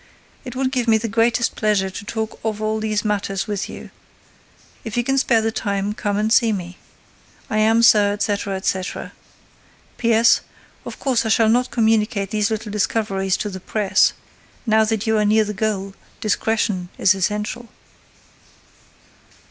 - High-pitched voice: Yes, high, 215 Hz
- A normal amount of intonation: No, narrow, 1.8 semitones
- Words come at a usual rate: Yes, average, 160 wpm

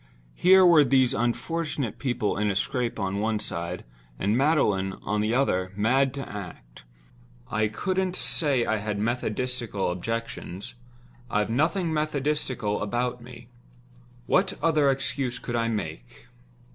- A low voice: Yes, low, 120 Hz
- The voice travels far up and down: No, average, 4.6 semitones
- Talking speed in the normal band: No, slow, 130 wpm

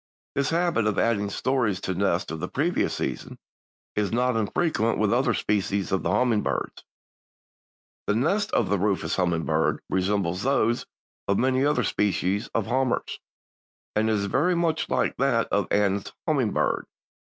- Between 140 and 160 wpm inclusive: Yes, average, 155 wpm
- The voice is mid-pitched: No, low, 105 Hz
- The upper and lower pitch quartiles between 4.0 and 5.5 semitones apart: Yes, average, 4.6 semitones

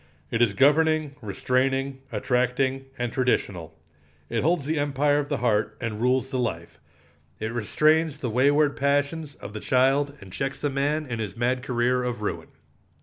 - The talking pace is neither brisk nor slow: Yes, average, 165 wpm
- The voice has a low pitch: Yes, low, 130 Hz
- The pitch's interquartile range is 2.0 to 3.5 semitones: Yes, average, 3.1 semitones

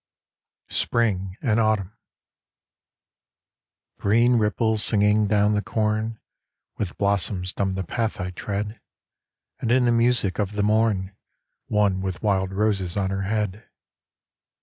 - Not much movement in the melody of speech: Yes, narrow, 2.2 semitones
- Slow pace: Yes, slow, 125 wpm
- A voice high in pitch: No, low, 105 Hz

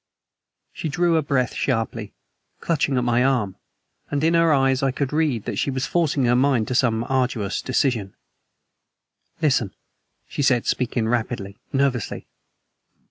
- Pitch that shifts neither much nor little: Yes, average, 3.0 semitones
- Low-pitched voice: Yes, low, 130 Hz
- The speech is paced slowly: No, average, 145 wpm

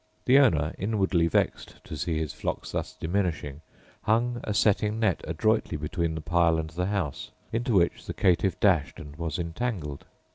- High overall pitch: No, very low, 85 Hz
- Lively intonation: No, average, 4.8 semitones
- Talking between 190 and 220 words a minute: No, average, 170 wpm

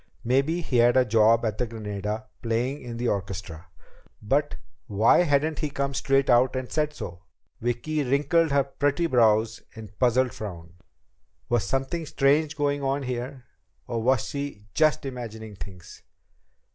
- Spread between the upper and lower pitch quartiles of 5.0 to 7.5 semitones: No, average, 4.2 semitones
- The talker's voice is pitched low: Yes, low, 125 Hz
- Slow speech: No, average, 155 wpm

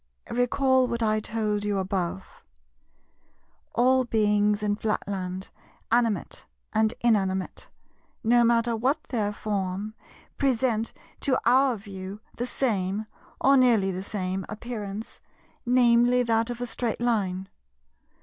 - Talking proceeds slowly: Yes, slow, 115 wpm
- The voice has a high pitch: Yes, high, 220 Hz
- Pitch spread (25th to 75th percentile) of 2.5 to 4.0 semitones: Yes, average, 3.2 semitones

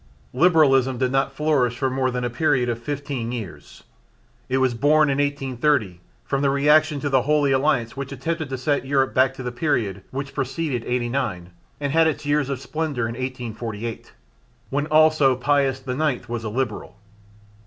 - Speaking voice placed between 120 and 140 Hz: Yes, low, 135 Hz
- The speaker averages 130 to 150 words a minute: No, average, 175 wpm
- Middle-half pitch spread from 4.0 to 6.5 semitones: No, average, 2.9 semitones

